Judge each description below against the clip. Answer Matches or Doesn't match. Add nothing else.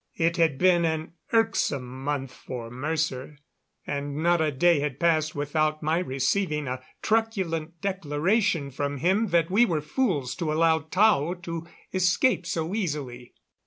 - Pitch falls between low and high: Matches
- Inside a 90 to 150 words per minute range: Matches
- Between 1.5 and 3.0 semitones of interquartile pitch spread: Doesn't match